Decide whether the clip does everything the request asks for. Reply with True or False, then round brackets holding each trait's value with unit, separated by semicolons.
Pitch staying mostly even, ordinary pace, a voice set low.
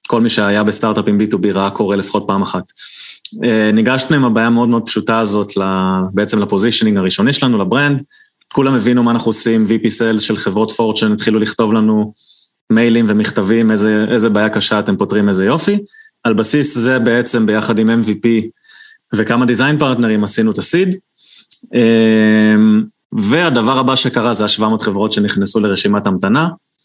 False (2.1 semitones; 155 wpm; 110 Hz)